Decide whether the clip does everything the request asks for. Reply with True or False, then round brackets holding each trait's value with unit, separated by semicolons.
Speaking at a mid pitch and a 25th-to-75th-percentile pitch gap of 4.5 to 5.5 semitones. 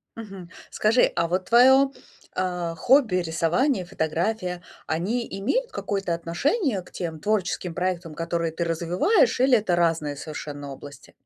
True (180 Hz; 5.1 semitones)